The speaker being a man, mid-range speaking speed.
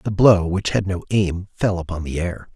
No: male; fast, 235 wpm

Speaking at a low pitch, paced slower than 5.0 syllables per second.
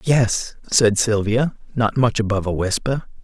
Yes: low, 115 Hz; 4.3 syllables/s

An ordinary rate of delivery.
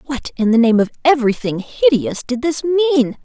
Yes: average, 185 wpm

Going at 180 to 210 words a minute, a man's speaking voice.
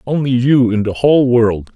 Yes: fast, 205 wpm; male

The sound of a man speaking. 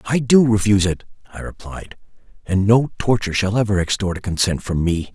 Yes: male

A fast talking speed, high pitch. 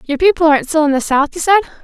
Yes: fast, 295 wpm; very high, 310 Hz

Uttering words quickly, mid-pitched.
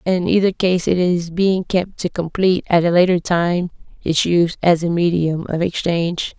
No: average, 190 wpm; medium, 175 Hz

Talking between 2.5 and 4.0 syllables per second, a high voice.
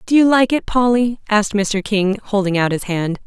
No: 5.0 syllables/s; high, 215 Hz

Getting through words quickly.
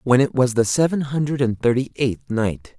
Yes: fast, 215 wpm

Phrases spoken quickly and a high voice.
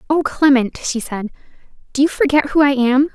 No: average, 190 wpm; very high, 275 Hz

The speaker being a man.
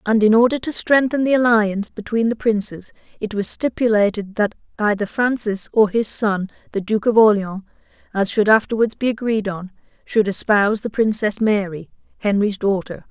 No: female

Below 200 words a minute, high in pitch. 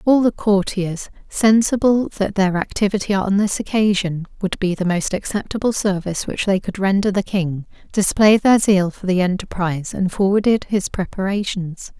Yes: average, 160 wpm; high, 195 Hz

